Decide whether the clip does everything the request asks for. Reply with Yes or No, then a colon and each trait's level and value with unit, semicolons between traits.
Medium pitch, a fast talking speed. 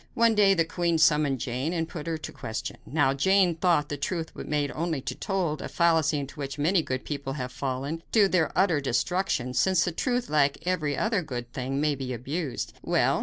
Yes: medium, 155 Hz; fast, 220 wpm